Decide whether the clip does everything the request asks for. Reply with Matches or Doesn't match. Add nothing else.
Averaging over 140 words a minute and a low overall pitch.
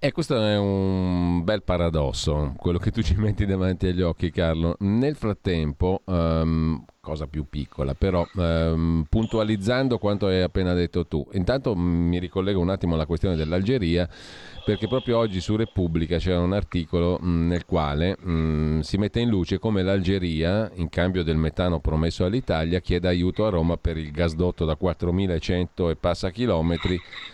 Matches